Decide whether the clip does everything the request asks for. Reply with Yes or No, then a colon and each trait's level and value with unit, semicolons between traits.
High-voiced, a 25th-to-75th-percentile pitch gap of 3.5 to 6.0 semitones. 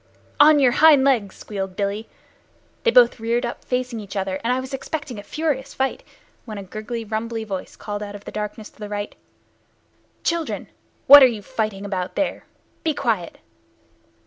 Yes: high, 225 Hz; average, 4.5 semitones